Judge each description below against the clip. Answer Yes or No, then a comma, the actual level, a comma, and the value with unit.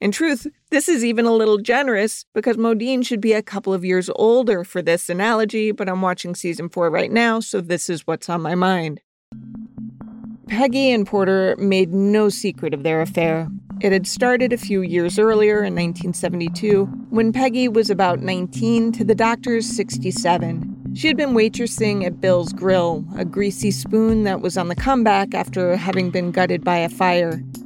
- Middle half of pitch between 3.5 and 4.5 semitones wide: Yes, average, 4.0 semitones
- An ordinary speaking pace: Yes, average, 180 wpm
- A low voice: No, high, 200 Hz